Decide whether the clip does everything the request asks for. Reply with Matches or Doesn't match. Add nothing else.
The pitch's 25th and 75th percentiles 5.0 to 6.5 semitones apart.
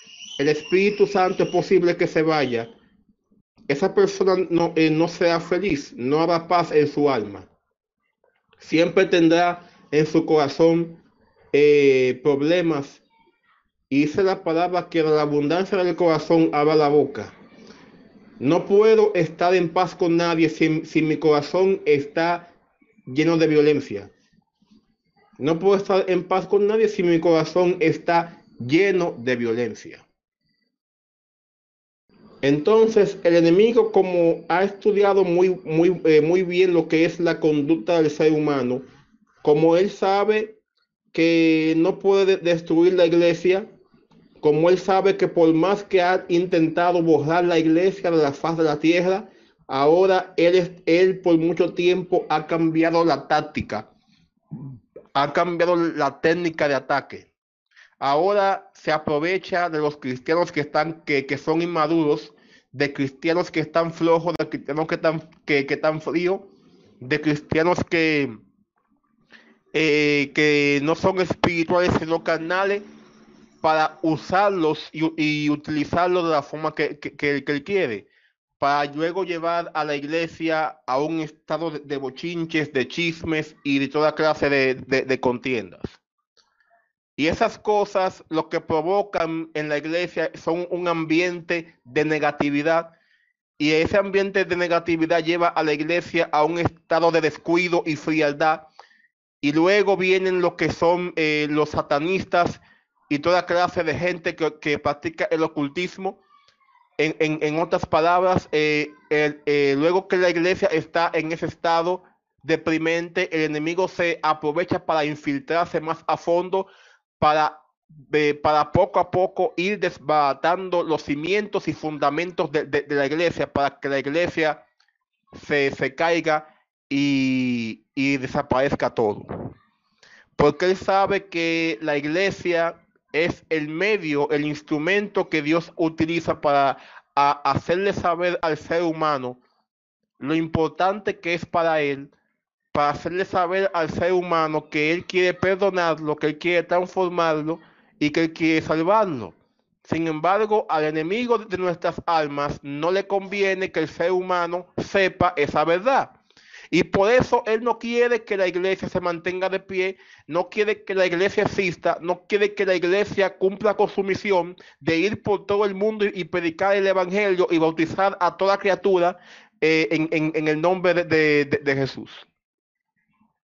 Doesn't match